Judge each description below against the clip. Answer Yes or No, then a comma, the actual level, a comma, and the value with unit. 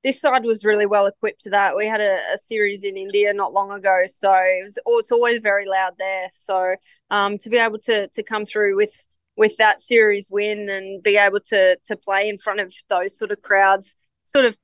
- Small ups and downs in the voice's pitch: Yes, narrow, 2.0 semitones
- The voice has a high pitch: Yes, high, 205 Hz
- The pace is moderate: No, fast, 225 wpm